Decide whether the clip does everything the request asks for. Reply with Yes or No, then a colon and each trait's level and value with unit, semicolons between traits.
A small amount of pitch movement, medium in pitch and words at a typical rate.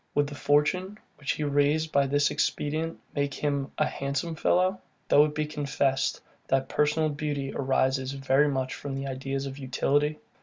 Yes: narrow, 1.7 semitones; medium, 145 Hz; average, 160 wpm